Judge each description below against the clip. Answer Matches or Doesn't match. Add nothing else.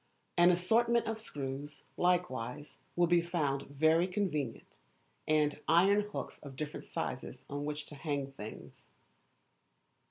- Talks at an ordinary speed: Doesn't match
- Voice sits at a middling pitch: Matches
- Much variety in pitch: Doesn't match